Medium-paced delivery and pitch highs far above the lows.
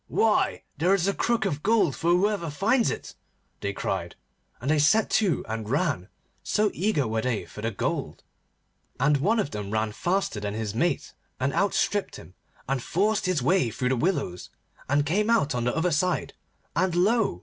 Yes: average, 185 wpm; wide, 8.9 semitones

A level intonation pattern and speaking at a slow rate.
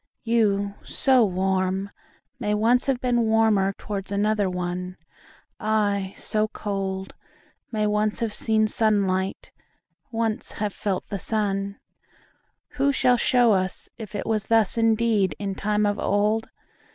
Yes: narrow, 2.3 semitones; slow, 115 wpm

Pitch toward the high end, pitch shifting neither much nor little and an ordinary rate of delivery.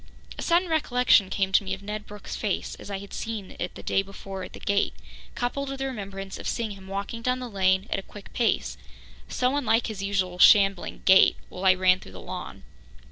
No: high, 200 Hz; average, 3.3 semitones; fast, 220 wpm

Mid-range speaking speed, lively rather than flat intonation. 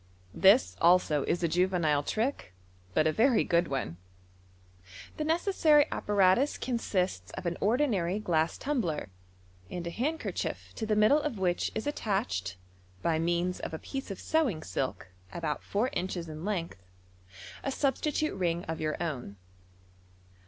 Yes: average, 145 wpm; wide, 6.9 semitones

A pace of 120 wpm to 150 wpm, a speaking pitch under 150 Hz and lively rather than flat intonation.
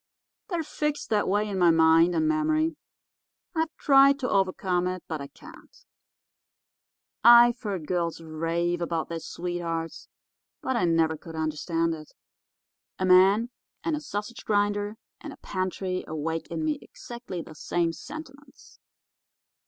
No: average, 140 wpm; medium, 185 Hz; wide, 6.7 semitones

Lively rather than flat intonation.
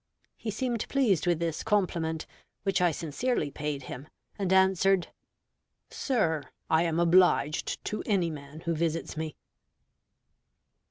No: average, 3.7 semitones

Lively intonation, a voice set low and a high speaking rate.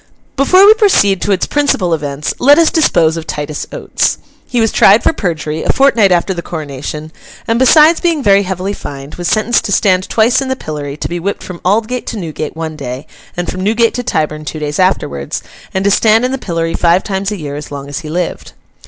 No: wide, 6.7 semitones; medium, 185 Hz; fast, 220 wpm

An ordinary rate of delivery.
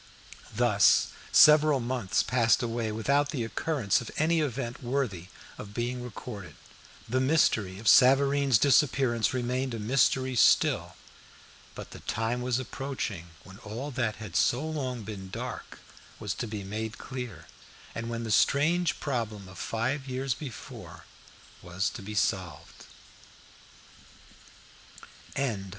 No: slow, 130 wpm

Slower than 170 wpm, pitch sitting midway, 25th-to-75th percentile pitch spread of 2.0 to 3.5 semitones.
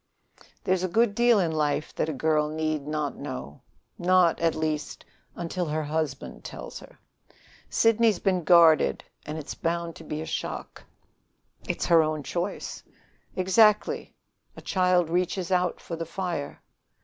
Yes: average, 150 wpm; medium, 165 Hz; average, 3.0 semitones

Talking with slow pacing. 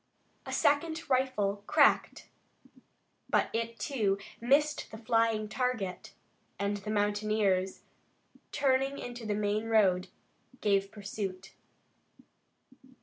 Yes: slow, 95 wpm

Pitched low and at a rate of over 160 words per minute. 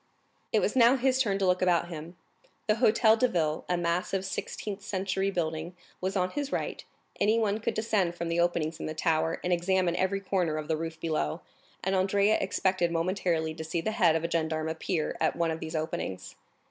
No: medium, 175 Hz; average, 200 wpm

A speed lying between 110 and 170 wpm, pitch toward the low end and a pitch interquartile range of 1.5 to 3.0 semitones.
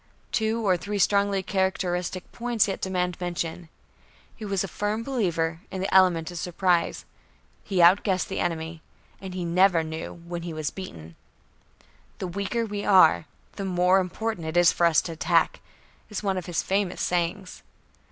No: average, 165 wpm; medium, 180 Hz; narrow, 2.6 semitones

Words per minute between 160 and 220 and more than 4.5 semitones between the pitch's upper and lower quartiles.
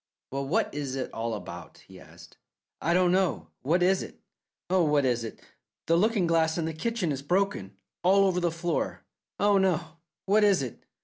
Yes: average, 190 wpm; wide, 5.5 semitones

